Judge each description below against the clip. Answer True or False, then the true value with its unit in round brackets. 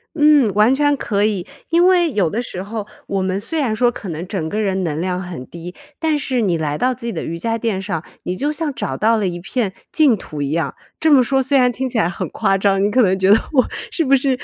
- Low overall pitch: False (215 Hz)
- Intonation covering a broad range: True (6.3 semitones)